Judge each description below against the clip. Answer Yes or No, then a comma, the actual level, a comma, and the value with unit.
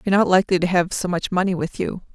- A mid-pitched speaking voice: Yes, medium, 180 Hz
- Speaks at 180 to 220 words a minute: No, fast, 280 wpm